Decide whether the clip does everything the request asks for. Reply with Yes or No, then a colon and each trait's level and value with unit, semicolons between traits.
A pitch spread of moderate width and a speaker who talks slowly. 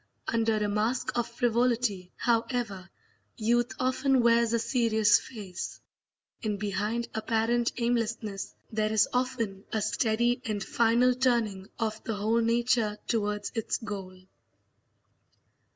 No: narrow, 2.2 semitones; slow, 120 wpm